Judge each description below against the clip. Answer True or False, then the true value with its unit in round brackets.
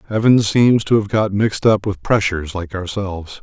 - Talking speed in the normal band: True (195 wpm)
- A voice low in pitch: True (100 Hz)